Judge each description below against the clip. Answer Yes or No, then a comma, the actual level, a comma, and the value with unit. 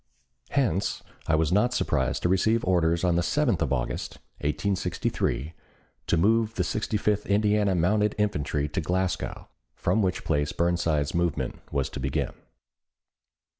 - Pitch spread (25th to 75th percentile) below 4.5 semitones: No, average, 5.1 semitones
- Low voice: Yes, very low, 90 Hz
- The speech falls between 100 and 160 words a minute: Yes, average, 140 wpm